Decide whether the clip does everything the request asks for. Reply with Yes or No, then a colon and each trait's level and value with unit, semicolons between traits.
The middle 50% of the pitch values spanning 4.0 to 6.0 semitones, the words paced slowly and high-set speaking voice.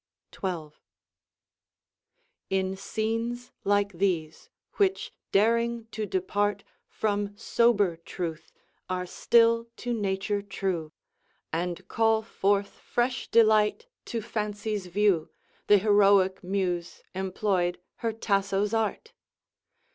No: average, 3.0 semitones; slow, 95 wpm; high, 205 Hz